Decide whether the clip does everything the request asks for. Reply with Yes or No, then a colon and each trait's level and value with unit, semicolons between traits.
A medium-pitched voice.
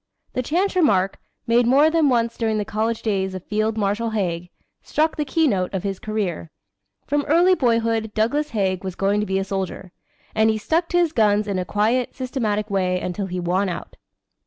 No: high, 215 Hz